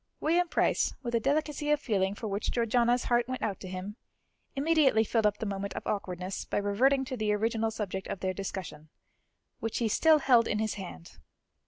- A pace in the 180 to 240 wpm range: Yes, average, 195 wpm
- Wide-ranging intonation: No, average, 4.5 semitones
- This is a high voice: Yes, high, 220 Hz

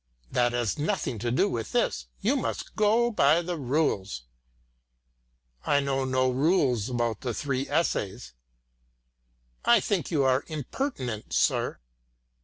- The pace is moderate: No, slow, 130 wpm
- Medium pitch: No, low, 130 Hz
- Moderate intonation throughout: Yes, average, 4.5 semitones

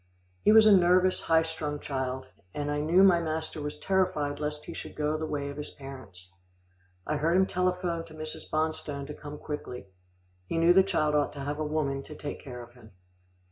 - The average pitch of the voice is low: No, medium, 150 Hz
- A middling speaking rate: No, fast, 210 wpm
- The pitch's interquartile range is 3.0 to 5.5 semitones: No, narrow, 2.6 semitones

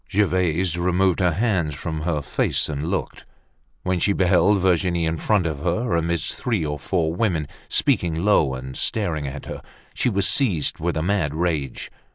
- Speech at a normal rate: Yes, average, 175 wpm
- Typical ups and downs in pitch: Yes, average, 3.5 semitones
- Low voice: Yes, very low, 85 Hz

